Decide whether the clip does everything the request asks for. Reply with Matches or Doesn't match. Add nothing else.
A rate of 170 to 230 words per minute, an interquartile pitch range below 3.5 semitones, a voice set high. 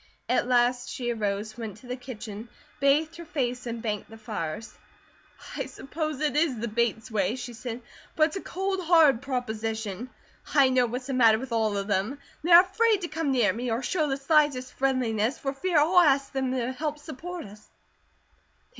Doesn't match